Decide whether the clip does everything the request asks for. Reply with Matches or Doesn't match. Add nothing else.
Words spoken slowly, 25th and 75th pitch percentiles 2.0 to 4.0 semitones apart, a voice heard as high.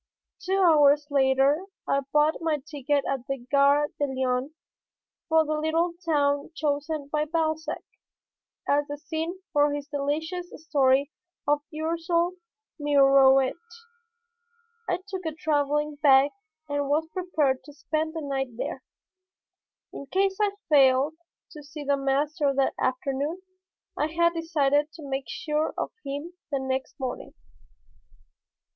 Matches